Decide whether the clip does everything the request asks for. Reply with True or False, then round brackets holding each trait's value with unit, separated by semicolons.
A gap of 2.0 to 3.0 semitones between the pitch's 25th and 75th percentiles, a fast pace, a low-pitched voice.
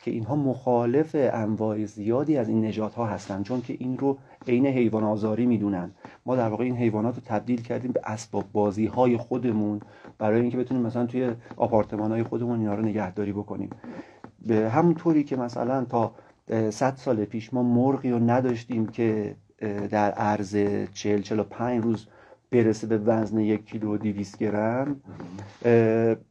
True (2.6 semitones; 160 wpm; 115 Hz)